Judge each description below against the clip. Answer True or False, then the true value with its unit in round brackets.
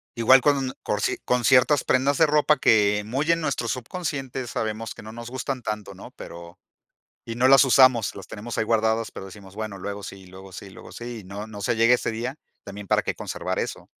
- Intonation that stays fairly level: False (4.1 semitones)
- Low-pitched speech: True (115 Hz)